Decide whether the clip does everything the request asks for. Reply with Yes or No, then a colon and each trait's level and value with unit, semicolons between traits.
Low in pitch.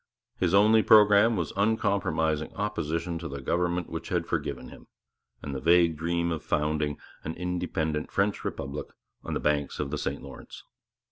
Yes: very low, 85 Hz